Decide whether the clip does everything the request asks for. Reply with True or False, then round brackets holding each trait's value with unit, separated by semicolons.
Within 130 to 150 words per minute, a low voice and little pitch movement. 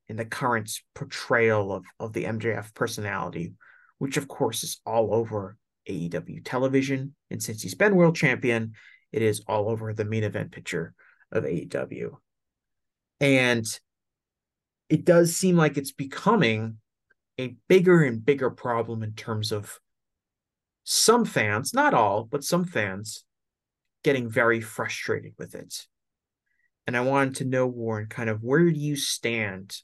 False (145 wpm; 115 Hz; 4.3 semitones)